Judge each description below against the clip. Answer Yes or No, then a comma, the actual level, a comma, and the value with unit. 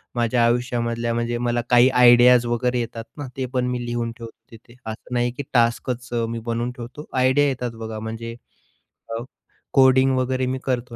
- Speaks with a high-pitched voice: No, low, 120 Hz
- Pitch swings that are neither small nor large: No, narrow, 1.4 semitones